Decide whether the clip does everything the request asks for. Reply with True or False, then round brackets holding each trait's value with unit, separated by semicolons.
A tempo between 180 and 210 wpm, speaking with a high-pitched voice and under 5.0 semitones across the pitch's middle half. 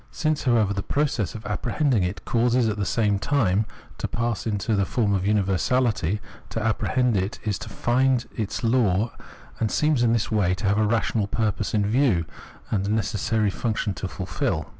False (185 wpm; 110 Hz; 3.1 semitones)